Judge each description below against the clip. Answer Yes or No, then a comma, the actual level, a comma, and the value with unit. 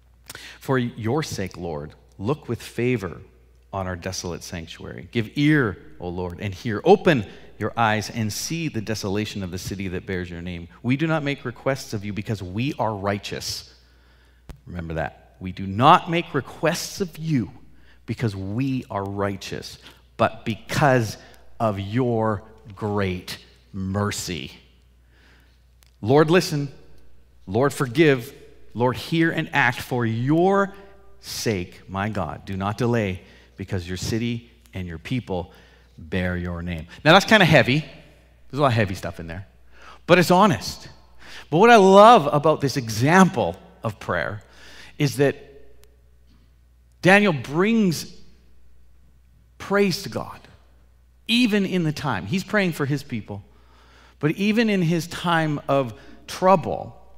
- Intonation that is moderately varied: No, wide, 8.7 semitones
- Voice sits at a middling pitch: No, low, 105 Hz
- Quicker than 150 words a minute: No, average, 140 wpm